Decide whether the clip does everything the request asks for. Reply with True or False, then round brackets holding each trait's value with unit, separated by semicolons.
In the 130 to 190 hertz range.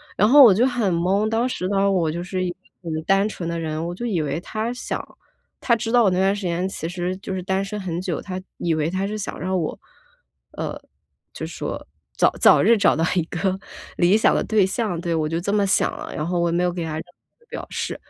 True (185 Hz)